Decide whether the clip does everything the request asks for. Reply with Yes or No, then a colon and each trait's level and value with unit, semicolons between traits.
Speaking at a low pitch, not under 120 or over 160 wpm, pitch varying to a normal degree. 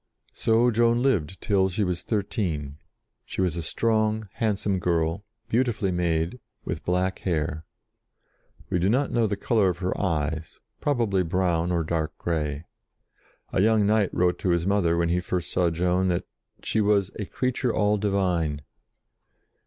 Yes: very low, 95 Hz; average, 155 wpm; average, 3.9 semitones